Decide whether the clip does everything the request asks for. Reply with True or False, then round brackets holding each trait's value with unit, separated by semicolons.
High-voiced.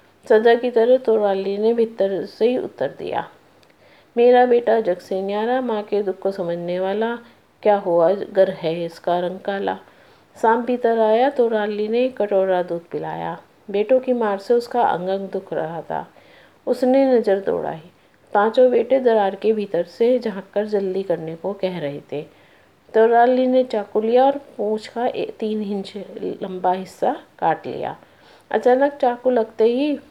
True (215 Hz)